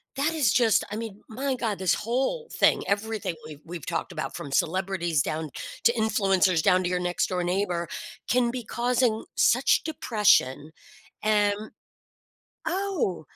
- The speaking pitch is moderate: No, high, 205 Hz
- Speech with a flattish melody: No, average, 5.2 semitones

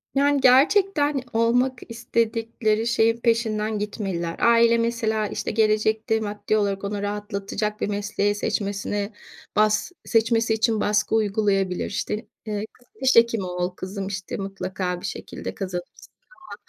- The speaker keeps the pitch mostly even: Yes, narrow, 2.3 semitones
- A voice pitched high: Yes, high, 215 Hz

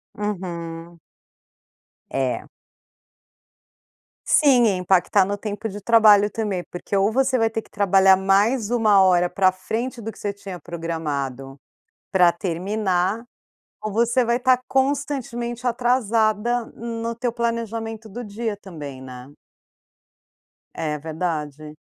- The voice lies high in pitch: Yes, high, 205 Hz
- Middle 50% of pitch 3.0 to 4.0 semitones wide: No, average, 4.7 semitones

